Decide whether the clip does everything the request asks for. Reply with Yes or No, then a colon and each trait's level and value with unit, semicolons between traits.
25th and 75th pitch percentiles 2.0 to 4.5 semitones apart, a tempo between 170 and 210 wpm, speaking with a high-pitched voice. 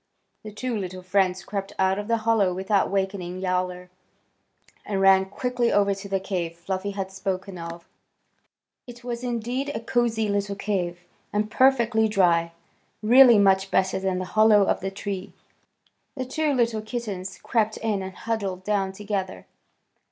No: average, 2.8 semitones; average, 155 wpm; high, 200 Hz